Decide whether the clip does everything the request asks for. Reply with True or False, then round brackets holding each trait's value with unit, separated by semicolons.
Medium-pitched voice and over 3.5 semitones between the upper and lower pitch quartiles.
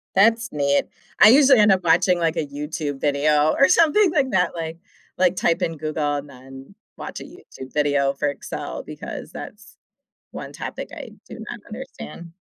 True (160 Hz; 5.5 semitones)